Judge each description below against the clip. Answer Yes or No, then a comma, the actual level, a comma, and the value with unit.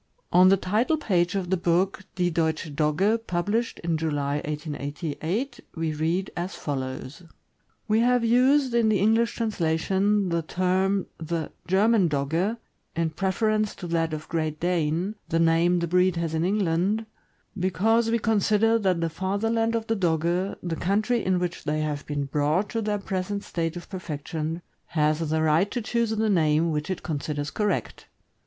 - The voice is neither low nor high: Yes, medium, 180 Hz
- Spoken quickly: No, average, 170 wpm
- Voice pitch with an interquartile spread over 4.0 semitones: Yes, average, 4.6 semitones